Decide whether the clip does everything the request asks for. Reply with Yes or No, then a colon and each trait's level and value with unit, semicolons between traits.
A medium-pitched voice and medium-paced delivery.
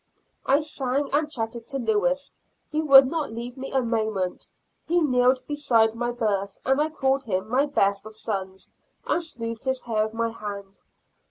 No: high, 240 Hz; average, 175 wpm